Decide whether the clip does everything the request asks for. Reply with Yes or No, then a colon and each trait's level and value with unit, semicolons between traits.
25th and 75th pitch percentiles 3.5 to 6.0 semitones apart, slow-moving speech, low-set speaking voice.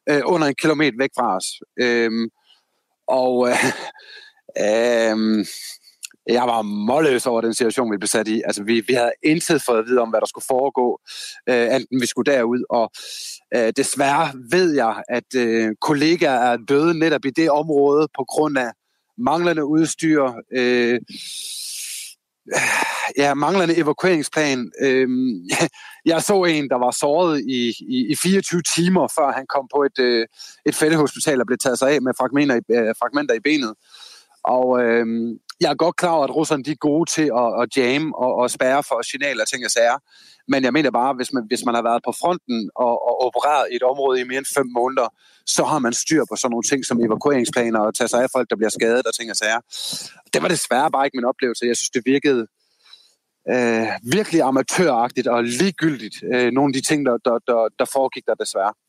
No: average, 4.3 semitones; average, 195 wpm; low, 130 Hz